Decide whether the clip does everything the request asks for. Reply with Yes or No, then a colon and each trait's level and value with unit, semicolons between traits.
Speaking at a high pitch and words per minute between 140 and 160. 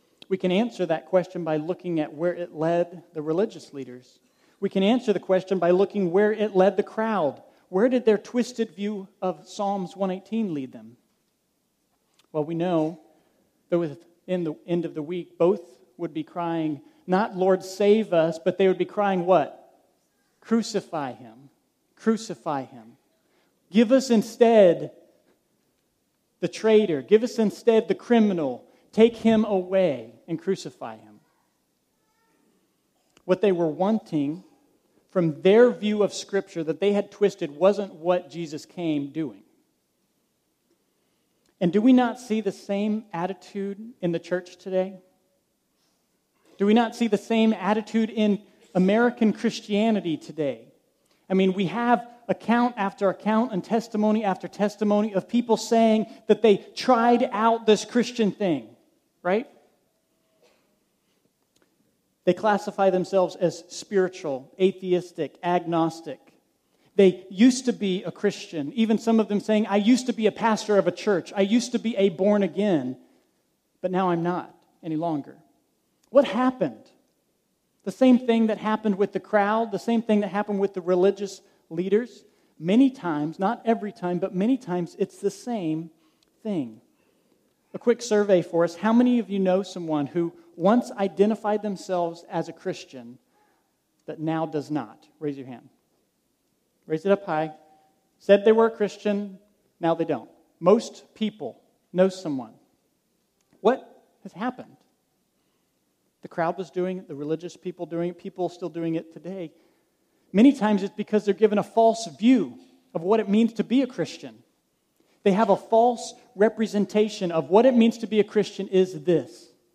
Yes: high, 195 Hz; average, 155 wpm